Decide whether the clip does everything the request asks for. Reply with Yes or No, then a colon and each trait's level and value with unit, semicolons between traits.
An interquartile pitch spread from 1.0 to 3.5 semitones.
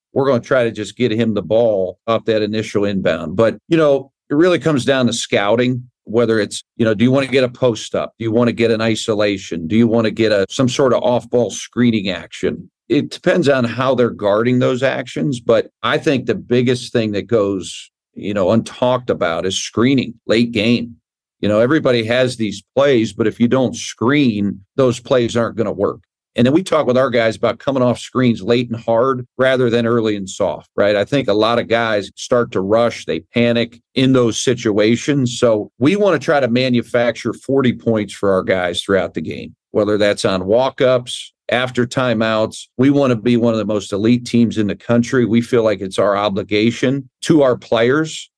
Yes: average, 2.7 semitones